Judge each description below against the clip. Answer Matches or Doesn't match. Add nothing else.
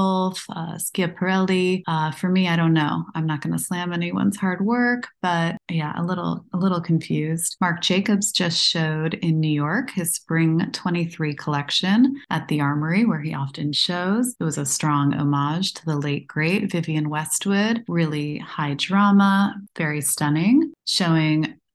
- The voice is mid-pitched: Matches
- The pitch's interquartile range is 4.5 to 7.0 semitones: Doesn't match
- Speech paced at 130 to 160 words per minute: Matches